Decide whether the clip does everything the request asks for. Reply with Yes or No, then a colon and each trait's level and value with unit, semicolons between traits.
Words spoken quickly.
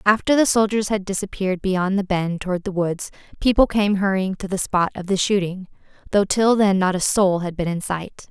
Yes: fast, 215 wpm